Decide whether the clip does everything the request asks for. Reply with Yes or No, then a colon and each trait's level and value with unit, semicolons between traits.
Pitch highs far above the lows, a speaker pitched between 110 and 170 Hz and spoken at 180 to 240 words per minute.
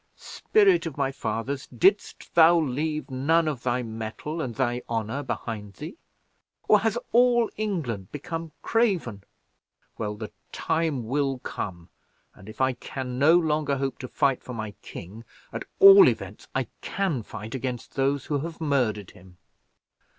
No: wide, 6.1 semitones; low, 135 Hz; average, 150 wpm